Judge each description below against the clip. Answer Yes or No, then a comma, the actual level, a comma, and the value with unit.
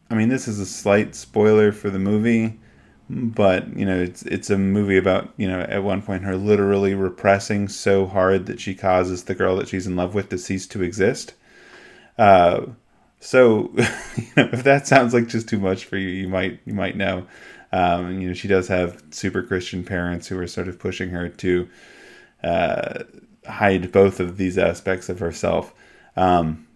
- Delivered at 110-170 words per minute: No, average, 190 wpm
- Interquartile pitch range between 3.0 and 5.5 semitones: No, narrow, 2.5 semitones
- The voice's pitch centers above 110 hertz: No, very low, 95 Hz